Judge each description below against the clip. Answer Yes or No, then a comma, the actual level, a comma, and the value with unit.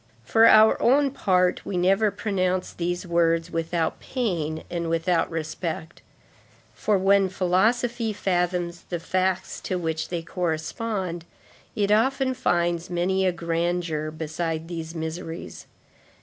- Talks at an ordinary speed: No, slow, 120 wpm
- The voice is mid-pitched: Yes, medium, 175 Hz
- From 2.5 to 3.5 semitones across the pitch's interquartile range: Yes, average, 2.8 semitones